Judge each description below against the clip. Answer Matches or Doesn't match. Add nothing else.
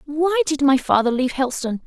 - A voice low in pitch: Doesn't match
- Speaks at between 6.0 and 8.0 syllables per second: Matches